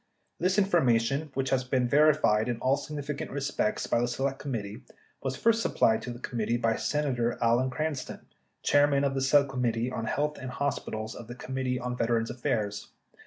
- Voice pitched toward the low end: Yes, low, 130 Hz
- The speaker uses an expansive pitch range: No, average, 3.3 semitones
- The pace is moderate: Yes, average, 180 wpm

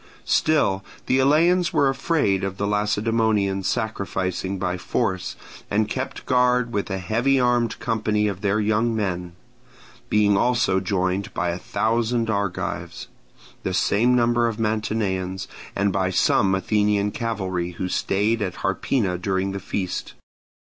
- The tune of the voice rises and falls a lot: No, average, 3.5 semitones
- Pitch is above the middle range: No, low, 105 Hz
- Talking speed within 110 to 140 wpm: Yes, slow, 135 wpm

